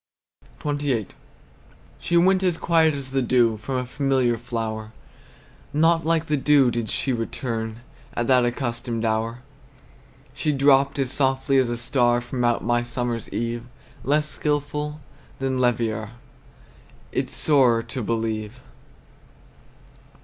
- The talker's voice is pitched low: Yes, low, 125 Hz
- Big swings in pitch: No, average, 3.5 semitones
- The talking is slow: Yes, slow, 125 wpm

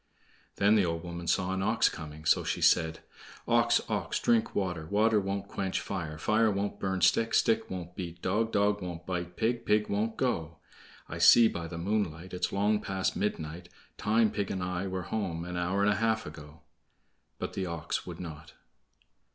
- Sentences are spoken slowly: No, average, 185 wpm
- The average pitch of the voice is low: Yes, very low, 95 Hz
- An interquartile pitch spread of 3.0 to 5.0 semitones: Yes, average, 3.5 semitones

